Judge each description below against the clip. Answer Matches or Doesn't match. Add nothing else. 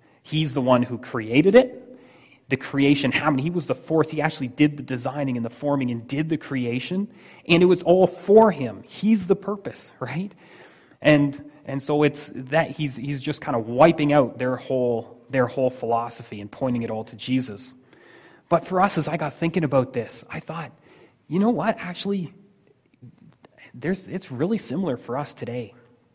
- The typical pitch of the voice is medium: Matches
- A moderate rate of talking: Matches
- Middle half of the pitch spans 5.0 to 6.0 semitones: Matches